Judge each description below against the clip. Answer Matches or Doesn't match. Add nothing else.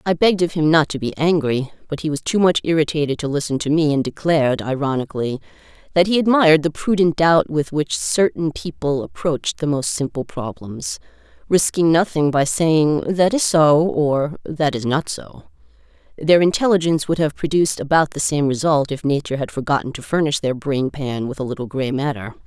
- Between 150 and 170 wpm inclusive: Doesn't match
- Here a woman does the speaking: Matches